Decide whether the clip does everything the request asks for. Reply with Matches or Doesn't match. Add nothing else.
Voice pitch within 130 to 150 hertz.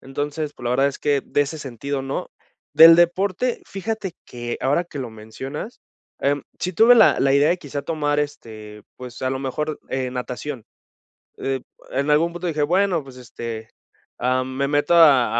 Matches